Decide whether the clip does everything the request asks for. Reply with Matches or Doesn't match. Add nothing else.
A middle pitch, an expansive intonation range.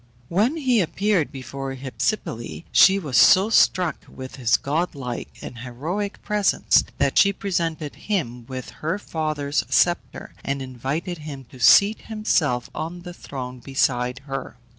Matches